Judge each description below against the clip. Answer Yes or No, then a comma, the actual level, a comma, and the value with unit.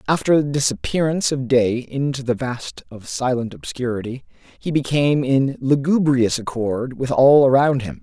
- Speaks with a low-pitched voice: Yes, low, 130 Hz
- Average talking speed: Yes, average, 150 wpm